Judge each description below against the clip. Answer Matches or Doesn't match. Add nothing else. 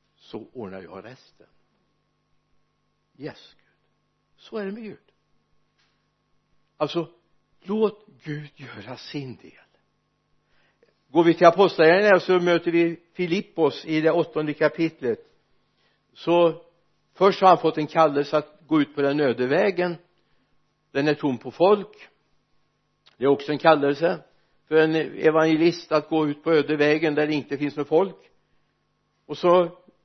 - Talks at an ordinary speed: Matches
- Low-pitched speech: Doesn't match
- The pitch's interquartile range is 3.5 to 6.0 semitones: Doesn't match